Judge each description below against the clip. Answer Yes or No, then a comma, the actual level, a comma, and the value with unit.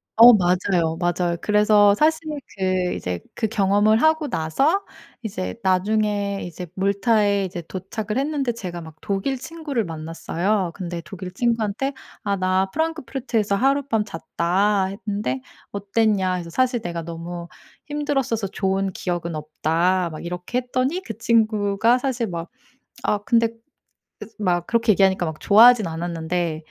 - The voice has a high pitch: Yes, high, 200 Hz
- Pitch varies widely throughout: No, average, 4.7 semitones